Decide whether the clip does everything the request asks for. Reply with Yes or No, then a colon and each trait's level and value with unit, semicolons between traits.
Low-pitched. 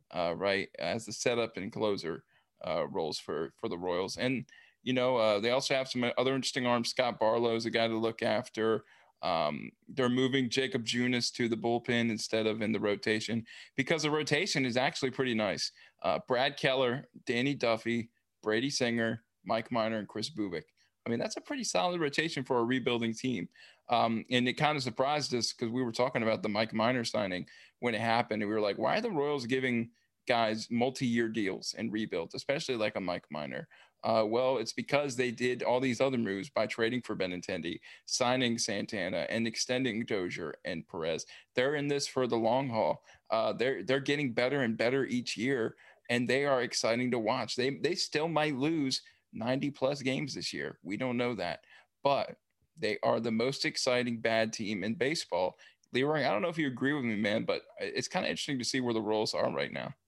Yes: low, 125 Hz